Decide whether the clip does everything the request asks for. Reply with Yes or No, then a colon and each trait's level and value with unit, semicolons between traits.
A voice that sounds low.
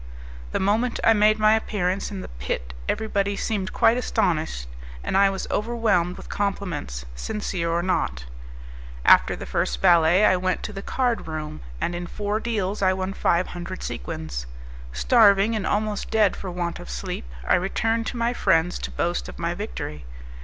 No: medium, 185 Hz